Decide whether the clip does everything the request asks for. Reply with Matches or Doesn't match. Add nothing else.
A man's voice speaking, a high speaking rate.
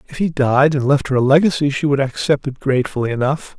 Matches